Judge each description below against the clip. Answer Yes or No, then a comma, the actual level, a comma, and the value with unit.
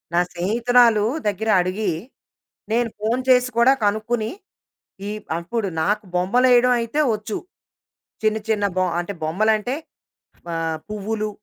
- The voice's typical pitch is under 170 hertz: No, high, 215 Hz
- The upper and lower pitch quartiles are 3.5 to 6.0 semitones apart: No, average, 2.8 semitones